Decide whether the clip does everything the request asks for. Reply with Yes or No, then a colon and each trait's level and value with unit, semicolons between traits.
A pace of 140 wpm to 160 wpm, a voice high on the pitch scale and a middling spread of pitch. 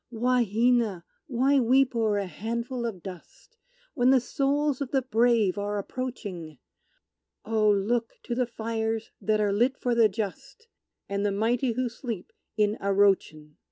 Yes: average, 150 wpm; high, 230 Hz; average, 3.5 semitones